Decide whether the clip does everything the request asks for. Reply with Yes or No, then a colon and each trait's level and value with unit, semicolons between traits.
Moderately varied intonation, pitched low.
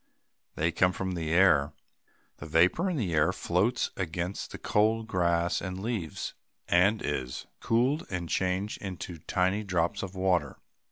Yes: average, 3.3 semitones; very low, 90 Hz